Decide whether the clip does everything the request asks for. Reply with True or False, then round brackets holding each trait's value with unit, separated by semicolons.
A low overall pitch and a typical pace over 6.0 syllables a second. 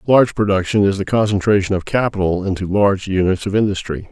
True (100 Hz; 6.3 syllables/s)